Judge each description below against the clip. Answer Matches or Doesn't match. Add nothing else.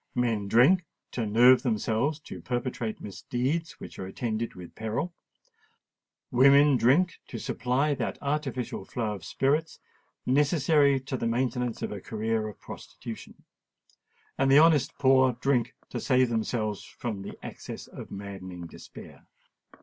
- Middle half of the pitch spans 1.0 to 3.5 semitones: Doesn't match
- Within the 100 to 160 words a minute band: Matches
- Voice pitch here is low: Matches